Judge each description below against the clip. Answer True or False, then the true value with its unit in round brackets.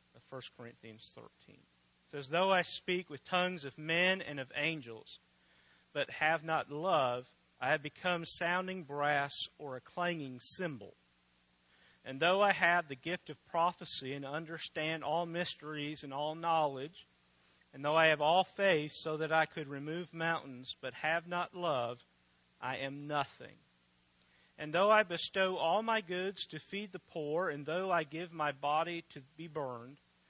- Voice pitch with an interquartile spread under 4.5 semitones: False (5.1 semitones)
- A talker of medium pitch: True (150 Hz)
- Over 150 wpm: True (160 wpm)